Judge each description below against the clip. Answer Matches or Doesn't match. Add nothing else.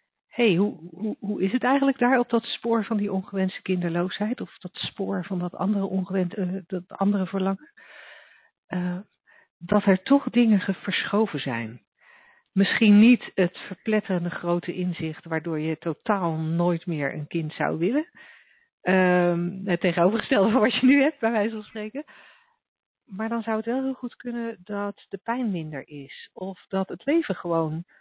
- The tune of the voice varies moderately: Matches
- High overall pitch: Matches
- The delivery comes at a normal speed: Matches